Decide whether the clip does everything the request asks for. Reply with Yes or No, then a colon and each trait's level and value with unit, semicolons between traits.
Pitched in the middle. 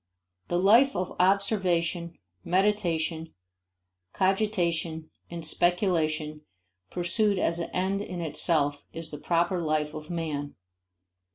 Yes: medium, 170 Hz